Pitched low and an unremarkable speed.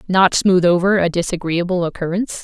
No: medium, 180 Hz; average, 150 wpm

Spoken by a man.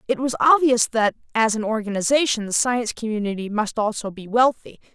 No: female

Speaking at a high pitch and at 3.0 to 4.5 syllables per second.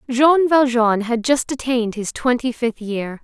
Yes: high, 245 Hz; 4.3 syllables/s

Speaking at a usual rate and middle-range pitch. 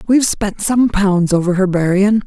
No: average, 185 wpm; high, 200 Hz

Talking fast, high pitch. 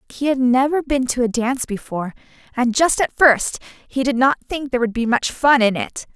Yes: fast, 225 wpm; very high, 255 Hz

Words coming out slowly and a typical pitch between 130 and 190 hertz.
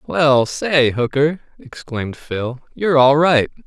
Yes: slow, 130 wpm; medium, 140 Hz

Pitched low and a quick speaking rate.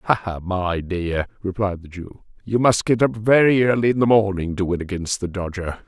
Yes: low, 100 Hz; fast, 215 wpm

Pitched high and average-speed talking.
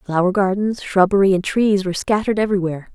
Yes: high, 195 Hz; average, 165 wpm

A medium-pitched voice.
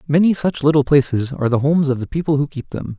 Yes: medium, 145 Hz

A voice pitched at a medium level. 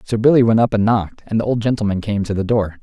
No: low, 110 Hz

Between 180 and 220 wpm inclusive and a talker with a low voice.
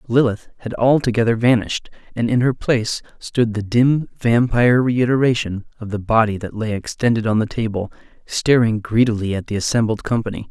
No: average, 160 wpm; low, 115 Hz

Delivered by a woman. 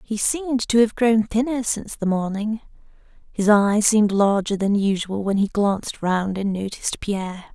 Yes: female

